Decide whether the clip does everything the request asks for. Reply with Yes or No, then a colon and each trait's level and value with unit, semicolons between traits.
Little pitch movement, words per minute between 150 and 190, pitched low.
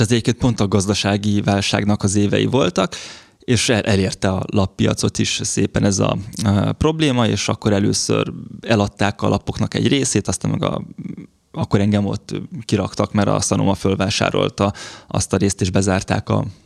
Yes: narrow, 2.3 semitones; fast, 155 wpm; low, 105 Hz